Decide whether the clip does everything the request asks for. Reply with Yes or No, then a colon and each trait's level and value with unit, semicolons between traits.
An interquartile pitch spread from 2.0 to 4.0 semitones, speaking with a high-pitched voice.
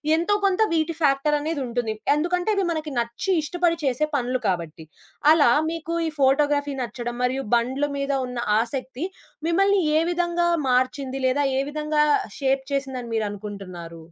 No: average, 4.6 semitones; very high, 275 Hz